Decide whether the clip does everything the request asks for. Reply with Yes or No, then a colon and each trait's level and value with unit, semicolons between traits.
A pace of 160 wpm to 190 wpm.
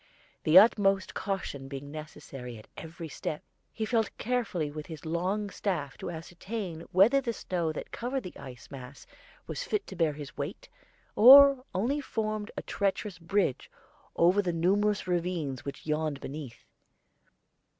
No: average, 150 wpm